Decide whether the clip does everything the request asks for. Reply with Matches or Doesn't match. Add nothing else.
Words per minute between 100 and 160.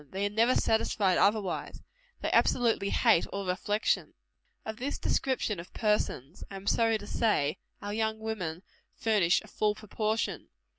Matches